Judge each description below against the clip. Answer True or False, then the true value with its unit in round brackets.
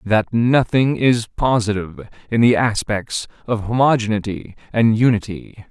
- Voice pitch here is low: True (110 Hz)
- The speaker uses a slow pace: True (115 wpm)